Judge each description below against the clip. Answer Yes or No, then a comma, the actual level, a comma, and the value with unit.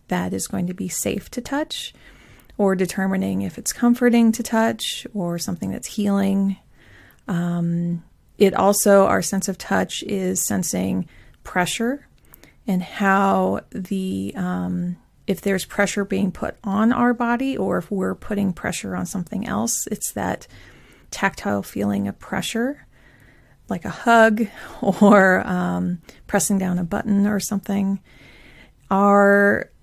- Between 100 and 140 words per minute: Yes, slow, 135 wpm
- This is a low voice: No, high, 195 Hz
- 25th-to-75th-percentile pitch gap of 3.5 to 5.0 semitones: No, narrow, 2.6 semitones